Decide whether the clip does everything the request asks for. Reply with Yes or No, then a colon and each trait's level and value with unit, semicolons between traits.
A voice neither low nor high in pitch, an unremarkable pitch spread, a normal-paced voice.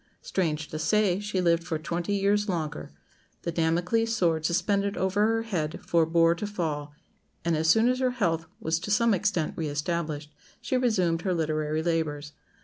Yes: medium, 170 Hz; average, 4.3 semitones; average, 170 wpm